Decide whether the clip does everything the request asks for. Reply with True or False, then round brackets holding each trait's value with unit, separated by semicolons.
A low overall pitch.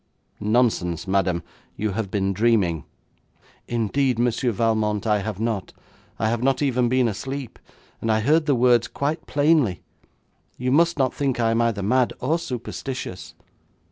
True (115 Hz)